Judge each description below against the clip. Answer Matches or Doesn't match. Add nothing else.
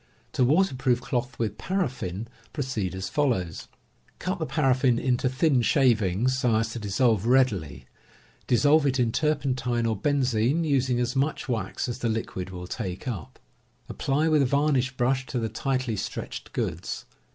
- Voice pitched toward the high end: Doesn't match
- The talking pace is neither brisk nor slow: Matches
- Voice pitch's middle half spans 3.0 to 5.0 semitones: Matches